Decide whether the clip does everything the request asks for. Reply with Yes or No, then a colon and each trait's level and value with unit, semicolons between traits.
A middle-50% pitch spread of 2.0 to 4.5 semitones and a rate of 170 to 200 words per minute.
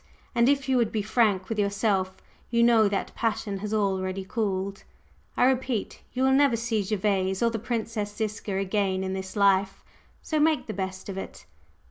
Yes: average, 3.3 semitones; average, 180 wpm